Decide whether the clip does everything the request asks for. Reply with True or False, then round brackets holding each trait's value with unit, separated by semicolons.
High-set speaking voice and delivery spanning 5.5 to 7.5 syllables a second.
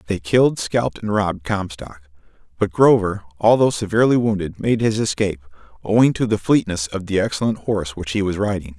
False (100 Hz; 5.8 syllables/s)